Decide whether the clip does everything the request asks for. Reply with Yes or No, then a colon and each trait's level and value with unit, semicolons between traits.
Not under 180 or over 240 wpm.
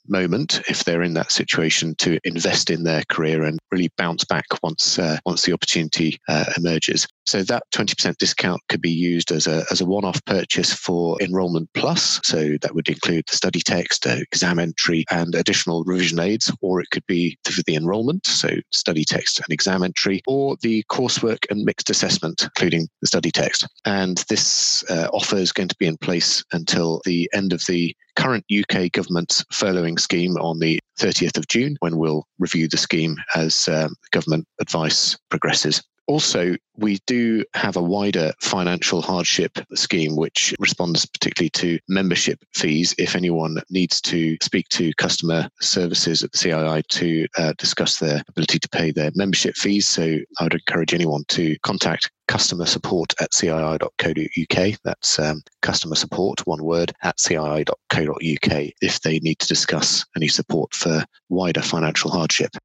No: average, 165 wpm